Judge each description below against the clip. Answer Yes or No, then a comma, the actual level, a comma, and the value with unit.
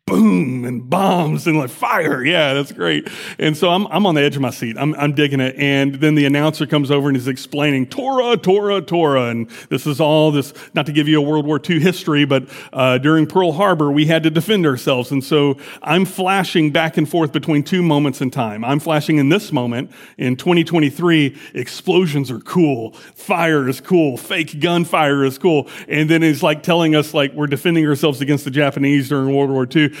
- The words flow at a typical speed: No, fast, 210 wpm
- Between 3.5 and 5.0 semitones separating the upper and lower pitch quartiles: No, average, 3.1 semitones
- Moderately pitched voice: Yes, medium, 150 Hz